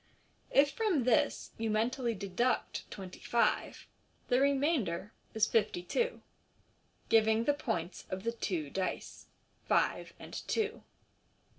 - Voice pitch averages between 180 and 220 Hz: No, high, 230 Hz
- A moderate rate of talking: No, slow, 125 wpm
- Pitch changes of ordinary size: No, wide, 6.2 semitones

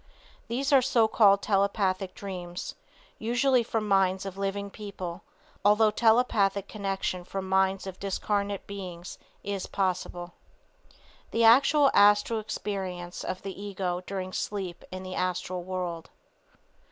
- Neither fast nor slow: No, slow, 125 wpm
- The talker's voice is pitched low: No, high, 195 Hz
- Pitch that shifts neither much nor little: No, narrow, 2.2 semitones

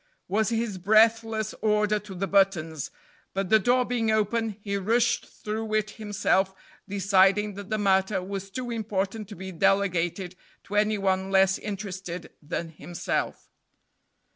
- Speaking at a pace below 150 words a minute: Yes, average, 140 wpm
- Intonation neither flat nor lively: No, narrow, 2.2 semitones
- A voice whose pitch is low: No, high, 200 Hz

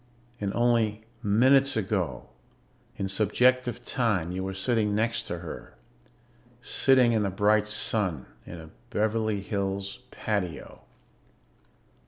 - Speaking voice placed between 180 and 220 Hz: No, low, 105 Hz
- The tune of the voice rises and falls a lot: No, average, 3.3 semitones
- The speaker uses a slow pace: Yes, slow, 115 wpm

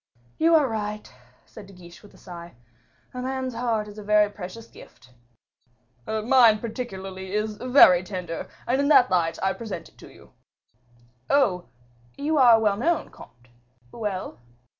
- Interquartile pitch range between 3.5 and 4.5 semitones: No, average, 4.9 semitones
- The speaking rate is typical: Yes, average, 155 wpm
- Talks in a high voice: Yes, high, 210 Hz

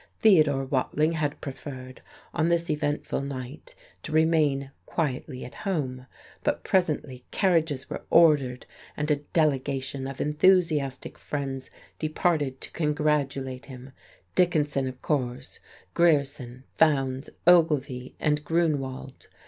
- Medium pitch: Yes, medium, 145 Hz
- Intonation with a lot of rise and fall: No, average, 3.0 semitones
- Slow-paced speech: Yes, slow, 110 wpm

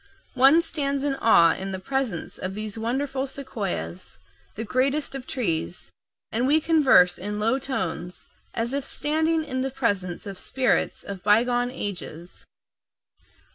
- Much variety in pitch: Yes, wide, 5.8 semitones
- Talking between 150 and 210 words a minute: No, average, 140 wpm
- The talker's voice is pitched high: Yes, high, 245 Hz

